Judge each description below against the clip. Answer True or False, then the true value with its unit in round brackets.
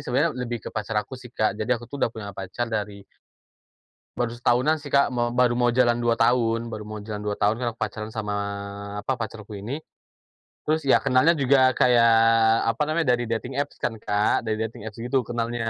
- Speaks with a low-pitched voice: True (115 Hz)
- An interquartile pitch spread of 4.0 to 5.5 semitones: False (2.7 semitones)